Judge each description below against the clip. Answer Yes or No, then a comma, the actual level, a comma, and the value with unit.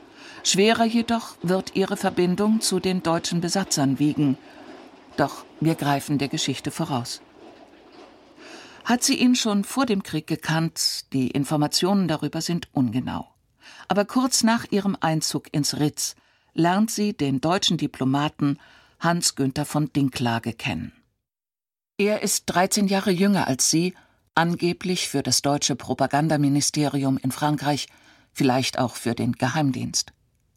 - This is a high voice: No, medium, 160 Hz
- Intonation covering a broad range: Yes, wide, 6.4 semitones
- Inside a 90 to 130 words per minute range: Yes, slow, 125 wpm